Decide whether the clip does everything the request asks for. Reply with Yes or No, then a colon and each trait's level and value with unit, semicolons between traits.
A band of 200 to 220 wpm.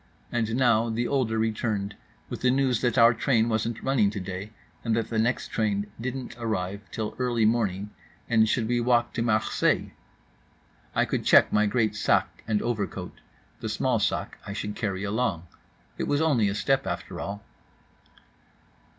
No: average, 160 wpm